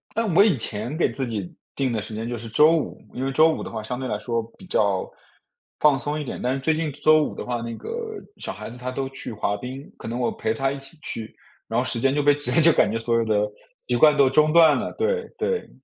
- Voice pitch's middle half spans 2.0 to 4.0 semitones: No, average, 4.7 semitones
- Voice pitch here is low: Yes, low, 130 Hz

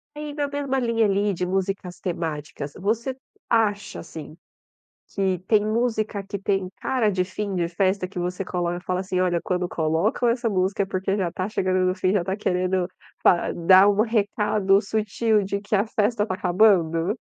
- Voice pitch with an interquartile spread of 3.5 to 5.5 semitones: No, average, 2.7 semitones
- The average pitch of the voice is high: Yes, high, 195 Hz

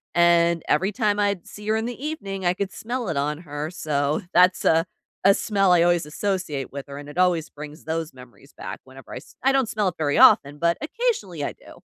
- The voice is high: No, medium, 175 Hz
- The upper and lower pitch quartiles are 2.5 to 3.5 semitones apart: No, average, 5.3 semitones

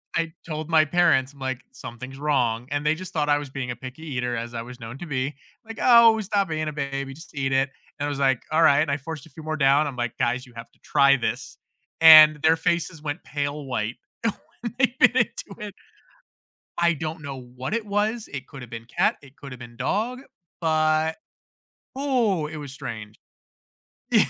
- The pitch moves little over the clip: No, average, 3.7 semitones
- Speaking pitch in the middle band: Yes, medium, 145 Hz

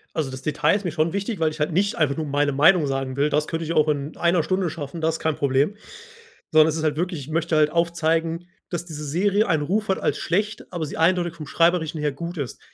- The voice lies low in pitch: No, medium, 160 Hz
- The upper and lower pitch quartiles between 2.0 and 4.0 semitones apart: Yes, narrow, 2.5 semitones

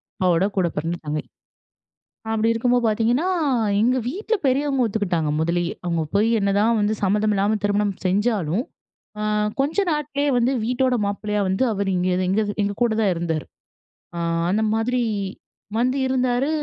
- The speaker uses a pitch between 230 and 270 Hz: No, high, 215 Hz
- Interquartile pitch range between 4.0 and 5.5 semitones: Yes, average, 4.7 semitones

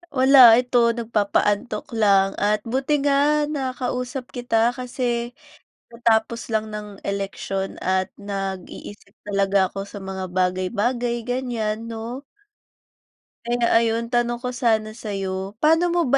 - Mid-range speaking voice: No, high, 230 Hz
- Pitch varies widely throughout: No, average, 3.7 semitones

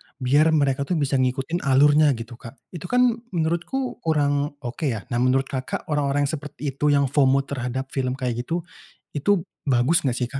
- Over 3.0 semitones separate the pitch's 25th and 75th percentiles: No, average, 2.7 semitones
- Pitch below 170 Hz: Yes, medium, 140 Hz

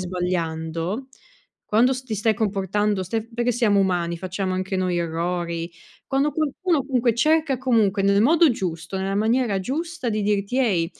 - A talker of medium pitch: No, high, 205 Hz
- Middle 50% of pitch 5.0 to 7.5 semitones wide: Yes, wide, 5.4 semitones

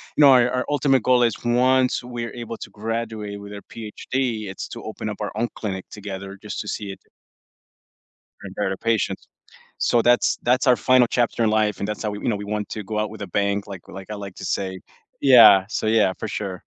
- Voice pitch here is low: Yes, low, 105 Hz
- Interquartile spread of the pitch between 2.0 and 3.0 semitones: Yes, average, 2.7 semitones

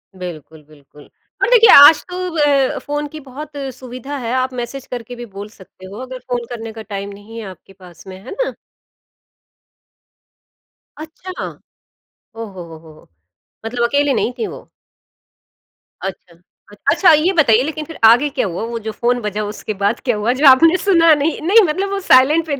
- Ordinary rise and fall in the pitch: No, wide, 6.1 semitones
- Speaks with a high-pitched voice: Yes, very high, 250 Hz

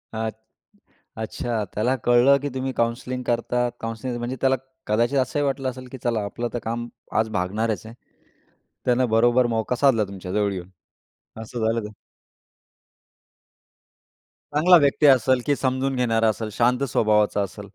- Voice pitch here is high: No, low, 120 Hz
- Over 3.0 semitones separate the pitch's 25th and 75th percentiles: No, average, 2.7 semitones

